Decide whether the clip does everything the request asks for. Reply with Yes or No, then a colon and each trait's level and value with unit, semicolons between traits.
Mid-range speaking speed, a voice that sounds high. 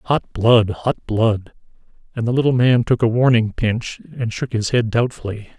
No: average, 185 wpm; low, 115 Hz